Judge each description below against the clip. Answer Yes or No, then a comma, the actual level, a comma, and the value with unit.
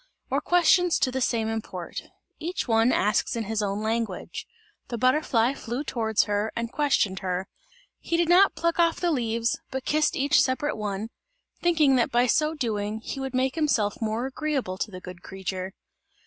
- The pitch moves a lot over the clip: Yes, wide, 5.7 semitones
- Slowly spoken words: No, average, 175 wpm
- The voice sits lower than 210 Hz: No, high, 235 Hz